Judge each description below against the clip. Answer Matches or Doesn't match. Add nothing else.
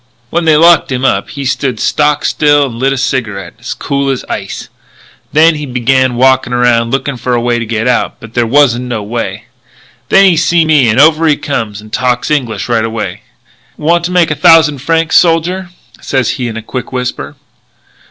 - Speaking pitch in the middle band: Doesn't match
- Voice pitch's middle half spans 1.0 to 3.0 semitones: Doesn't match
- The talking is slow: Doesn't match